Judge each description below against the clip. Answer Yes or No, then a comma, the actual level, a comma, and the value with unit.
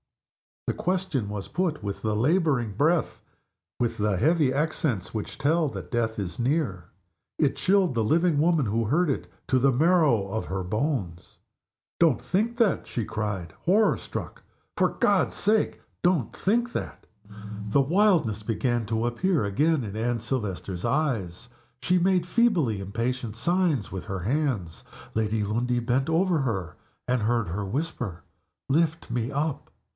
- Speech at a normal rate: Yes, average, 150 wpm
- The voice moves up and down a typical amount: No, wide, 7.3 semitones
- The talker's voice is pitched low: Yes, low, 125 Hz